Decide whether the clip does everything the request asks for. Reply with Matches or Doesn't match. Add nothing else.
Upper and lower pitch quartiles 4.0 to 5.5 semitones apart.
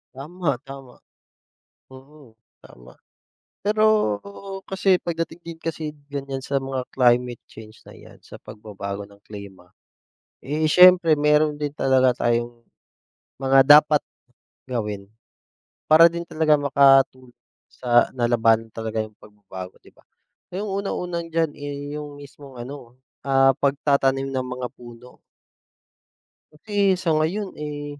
Matches